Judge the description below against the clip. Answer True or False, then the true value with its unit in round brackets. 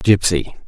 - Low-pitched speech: True (95 Hz)